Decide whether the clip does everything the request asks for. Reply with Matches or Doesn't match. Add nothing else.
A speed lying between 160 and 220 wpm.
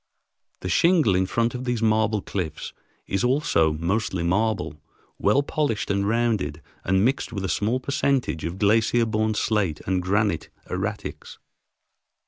Doesn't match